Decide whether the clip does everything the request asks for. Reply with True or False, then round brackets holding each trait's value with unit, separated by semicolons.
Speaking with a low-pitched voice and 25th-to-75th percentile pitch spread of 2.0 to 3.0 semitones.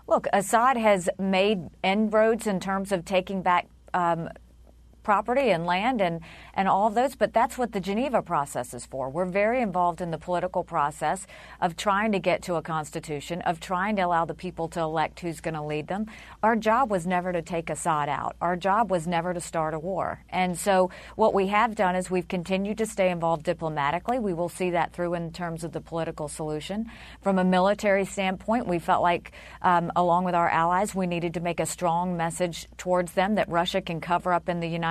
False (180 Hz; 2.7 semitones)